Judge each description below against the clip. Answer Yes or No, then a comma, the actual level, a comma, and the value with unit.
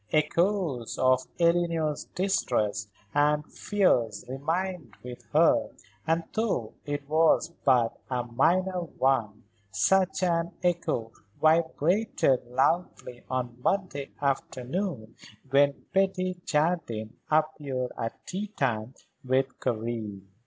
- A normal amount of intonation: No, wide, 5.9 semitones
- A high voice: No, medium, 145 Hz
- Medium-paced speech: No, slow, 100 wpm